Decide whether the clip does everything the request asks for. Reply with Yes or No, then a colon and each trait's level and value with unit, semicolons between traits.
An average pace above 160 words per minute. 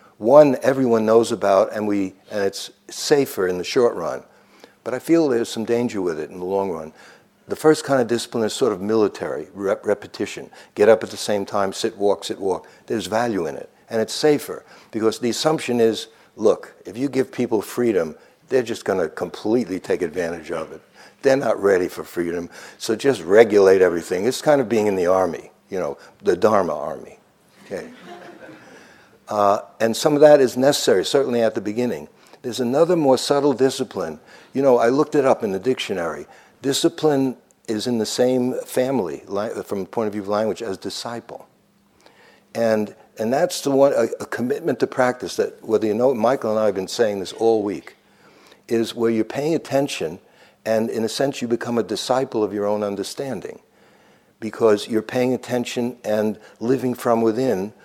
Yes: average, 190 wpm